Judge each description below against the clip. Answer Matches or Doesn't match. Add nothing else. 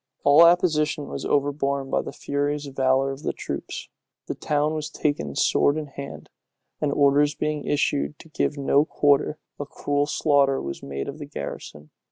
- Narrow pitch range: Matches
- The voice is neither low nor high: Matches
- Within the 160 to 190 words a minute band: Matches